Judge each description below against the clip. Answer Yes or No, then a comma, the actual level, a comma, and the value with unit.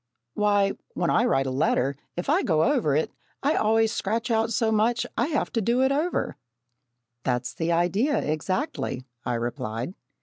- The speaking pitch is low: No, high, 205 Hz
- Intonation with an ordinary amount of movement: No, wide, 7.7 semitones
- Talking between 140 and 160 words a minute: No, average, 175 wpm